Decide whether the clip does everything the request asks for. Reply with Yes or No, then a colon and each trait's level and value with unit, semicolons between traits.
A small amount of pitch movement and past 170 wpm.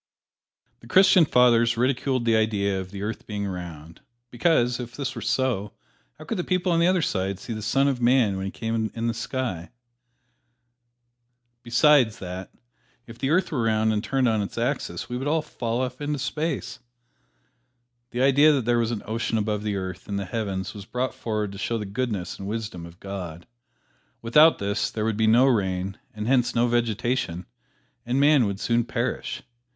No: average, 4.1 semitones; average, 190 wpm